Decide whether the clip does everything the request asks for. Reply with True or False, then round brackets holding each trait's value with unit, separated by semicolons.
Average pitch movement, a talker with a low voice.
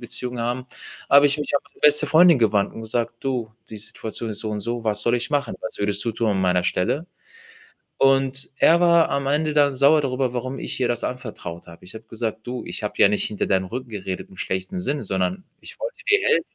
True (4.9 semitones; 120 Hz)